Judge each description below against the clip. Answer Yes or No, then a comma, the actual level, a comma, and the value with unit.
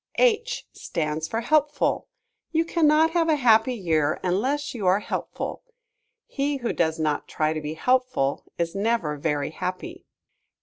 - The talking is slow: No, average, 145 wpm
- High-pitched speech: Yes, high, 220 Hz